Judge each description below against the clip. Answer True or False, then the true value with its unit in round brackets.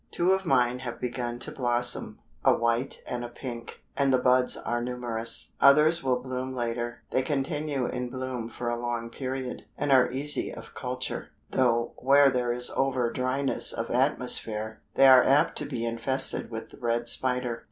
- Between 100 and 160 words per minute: False (175 wpm)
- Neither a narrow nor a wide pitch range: False (1.9 semitones)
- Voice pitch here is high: False (125 Hz)